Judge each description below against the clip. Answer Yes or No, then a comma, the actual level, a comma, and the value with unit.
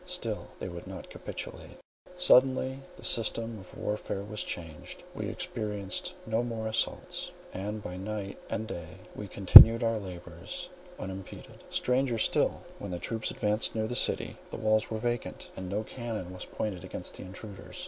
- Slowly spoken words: No, average, 160 wpm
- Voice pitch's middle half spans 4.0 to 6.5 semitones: No, average, 3.3 semitones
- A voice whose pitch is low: Yes, low, 105 Hz